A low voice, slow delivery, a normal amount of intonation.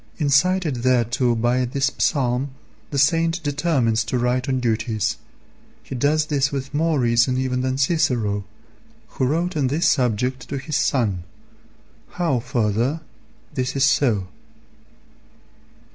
Yes: low, 130 Hz; slow, 130 wpm; average, 3.3 semitones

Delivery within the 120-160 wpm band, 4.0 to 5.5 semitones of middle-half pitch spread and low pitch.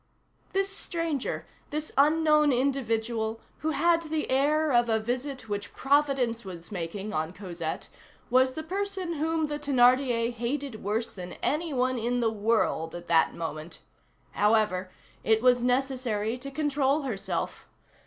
No: average, 140 wpm; average, 5.2 semitones; very high, 250 Hz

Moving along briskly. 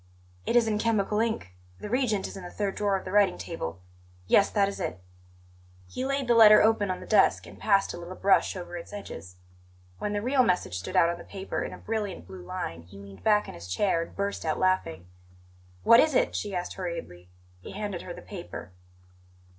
Yes: fast, 215 wpm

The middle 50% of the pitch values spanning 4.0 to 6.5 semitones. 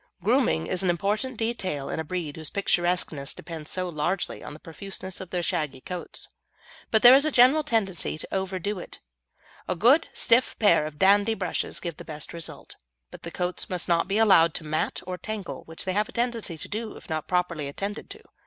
Yes: average, 4.5 semitones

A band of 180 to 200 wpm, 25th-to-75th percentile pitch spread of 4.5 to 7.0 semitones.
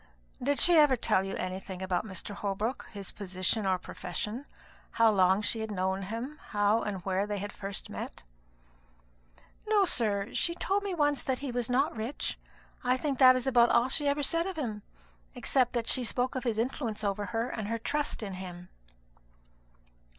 Yes: average, 185 wpm; average, 4.9 semitones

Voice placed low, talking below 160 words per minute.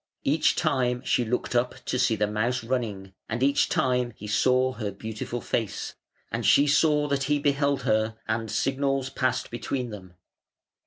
No: low, 125 Hz; average, 165 wpm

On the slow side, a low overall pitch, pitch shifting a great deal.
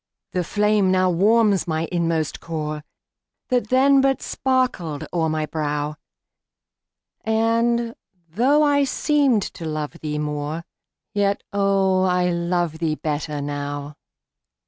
No: slow, 120 wpm; medium, 180 Hz; wide, 6.5 semitones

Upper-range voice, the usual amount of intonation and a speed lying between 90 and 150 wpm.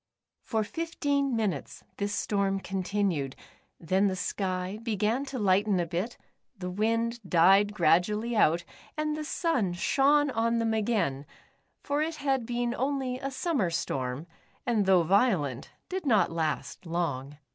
No: high, 210 Hz; wide, 5.8 semitones; average, 140 wpm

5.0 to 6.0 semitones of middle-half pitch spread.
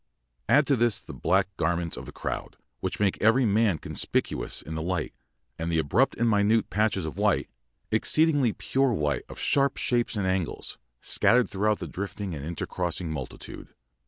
Yes: wide, 5.6 semitones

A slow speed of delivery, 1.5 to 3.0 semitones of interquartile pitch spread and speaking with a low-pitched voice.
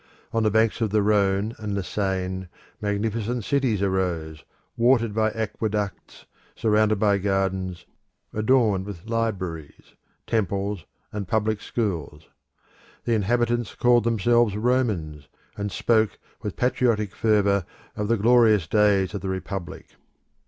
Yes: slow, 125 wpm; average, 2.7 semitones; low, 105 Hz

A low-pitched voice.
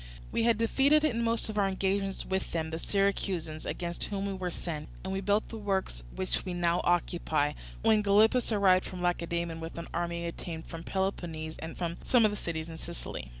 No: medium, 185 Hz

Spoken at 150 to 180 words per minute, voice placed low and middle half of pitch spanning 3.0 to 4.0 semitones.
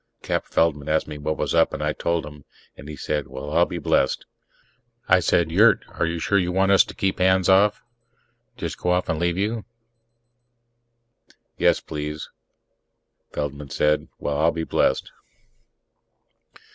Yes: average, 160 wpm; very low, 80 Hz; average, 3.6 semitones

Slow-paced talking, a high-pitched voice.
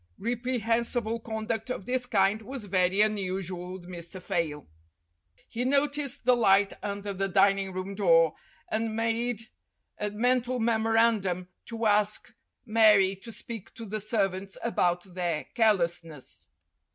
Yes: slow, 130 wpm; high, 210 Hz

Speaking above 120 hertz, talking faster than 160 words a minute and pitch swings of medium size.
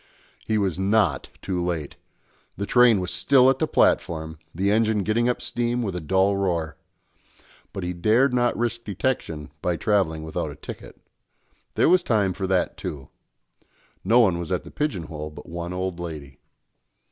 No: very low, 95 Hz; average, 170 wpm; average, 4.8 semitones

